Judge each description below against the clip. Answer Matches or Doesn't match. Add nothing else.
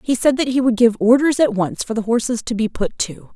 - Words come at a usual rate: Doesn't match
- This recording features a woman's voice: Matches